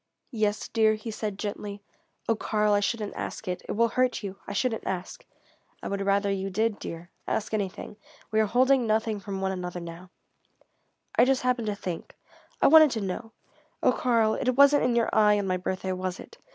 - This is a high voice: Yes, high, 210 Hz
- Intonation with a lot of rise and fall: No, average, 3.0 semitones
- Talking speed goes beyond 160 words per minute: Yes, average, 200 wpm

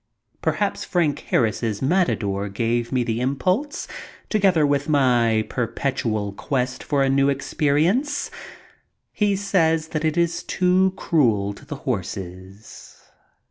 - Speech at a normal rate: No, slow, 120 wpm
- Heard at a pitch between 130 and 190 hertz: Yes, medium, 140 Hz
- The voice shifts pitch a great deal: Yes, wide, 6.8 semitones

